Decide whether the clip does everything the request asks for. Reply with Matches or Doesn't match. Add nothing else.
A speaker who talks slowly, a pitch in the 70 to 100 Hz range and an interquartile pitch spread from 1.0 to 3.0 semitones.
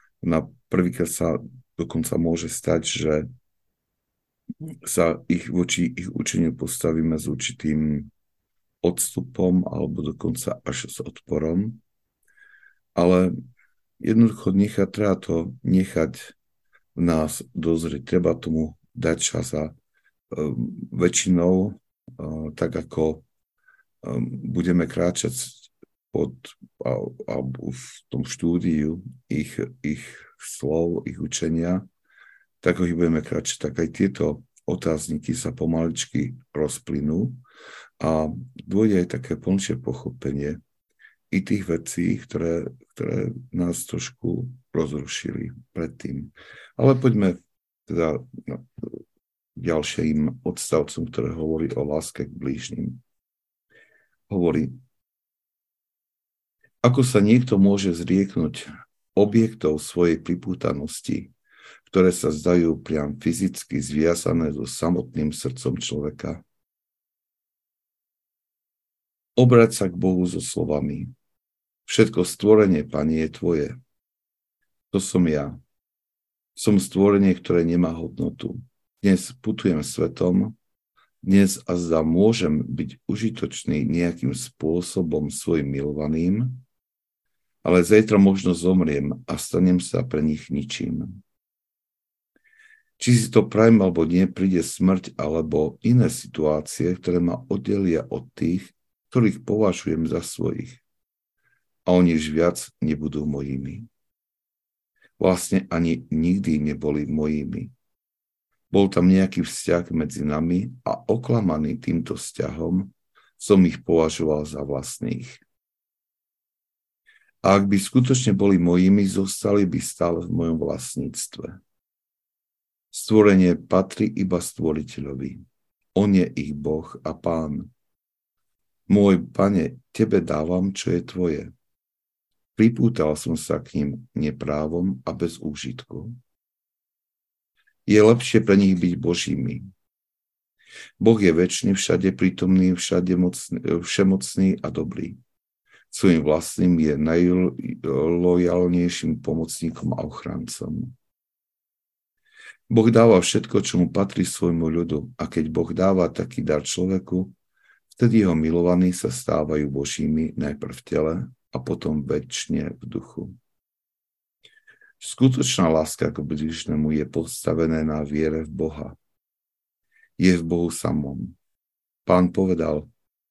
Doesn't match